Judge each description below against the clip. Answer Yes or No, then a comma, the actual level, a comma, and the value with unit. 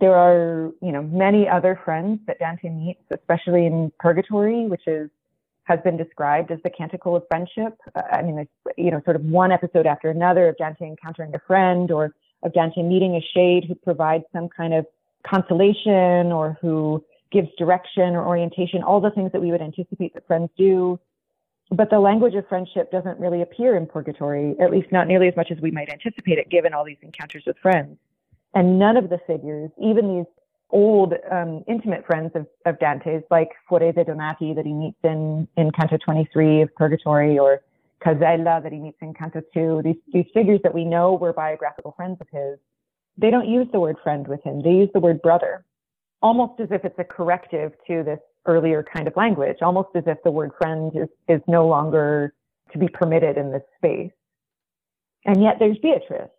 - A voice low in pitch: No, medium, 170 Hz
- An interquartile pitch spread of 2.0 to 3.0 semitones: Yes, narrow, 2.6 semitones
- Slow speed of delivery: No, average, 200 wpm